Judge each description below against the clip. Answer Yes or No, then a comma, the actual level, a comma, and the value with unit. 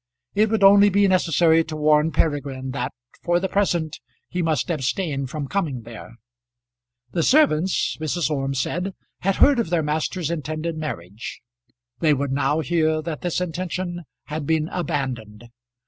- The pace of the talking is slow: No, average, 150 wpm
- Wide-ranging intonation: No, average, 3.9 semitones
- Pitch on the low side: No, medium, 160 Hz